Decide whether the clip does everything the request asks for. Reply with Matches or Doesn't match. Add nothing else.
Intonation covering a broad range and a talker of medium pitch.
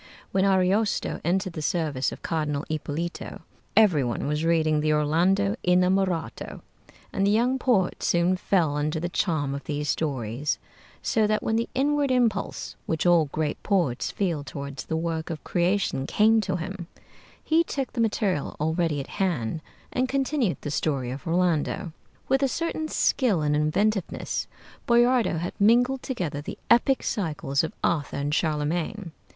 Matches